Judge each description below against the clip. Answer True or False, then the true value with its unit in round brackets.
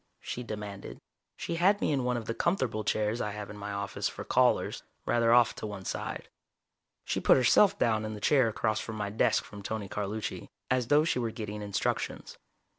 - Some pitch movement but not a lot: True (3.0 semitones)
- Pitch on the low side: True (110 Hz)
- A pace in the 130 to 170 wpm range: False (195 wpm)